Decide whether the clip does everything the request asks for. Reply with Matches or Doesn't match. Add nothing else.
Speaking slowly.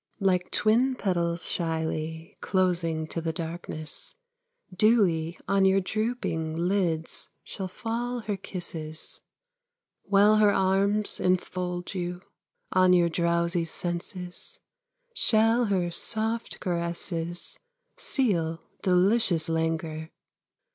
Matches